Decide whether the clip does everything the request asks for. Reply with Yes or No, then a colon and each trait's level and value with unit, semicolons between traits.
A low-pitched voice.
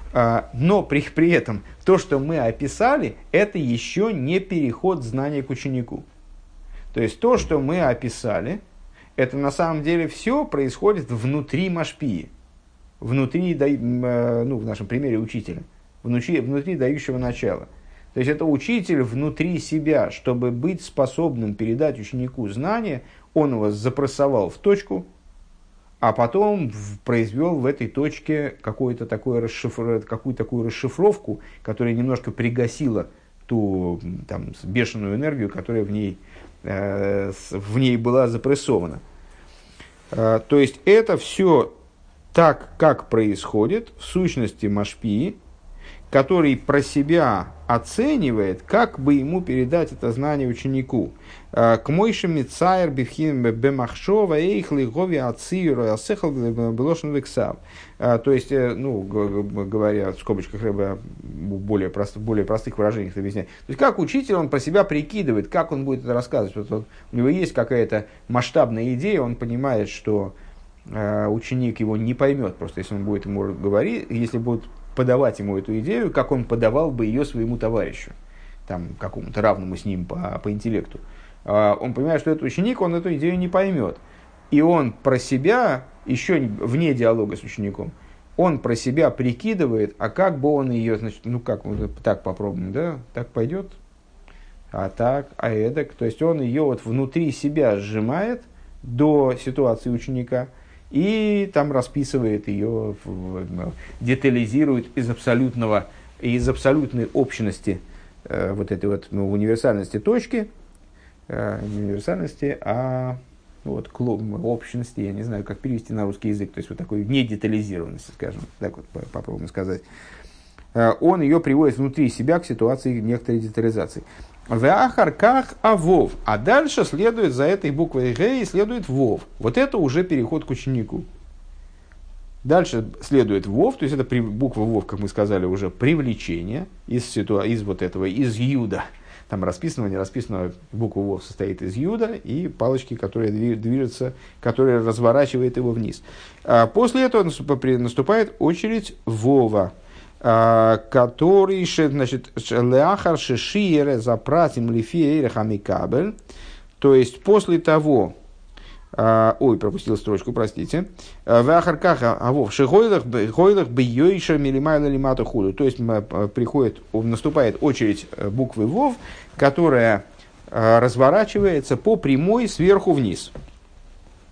Yes: low, 120 Hz